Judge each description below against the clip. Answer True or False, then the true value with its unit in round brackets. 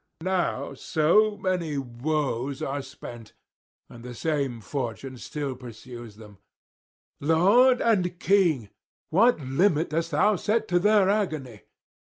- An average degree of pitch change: False (6.8 semitones)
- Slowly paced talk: True (120 wpm)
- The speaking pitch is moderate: True (150 Hz)